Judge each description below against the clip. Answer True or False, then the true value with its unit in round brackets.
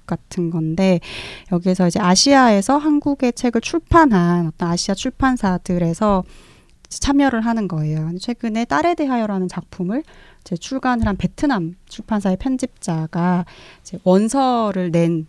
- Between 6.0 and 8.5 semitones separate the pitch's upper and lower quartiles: True (6.4 semitones)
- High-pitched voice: True (195 Hz)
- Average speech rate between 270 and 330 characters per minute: True (290 characters per minute)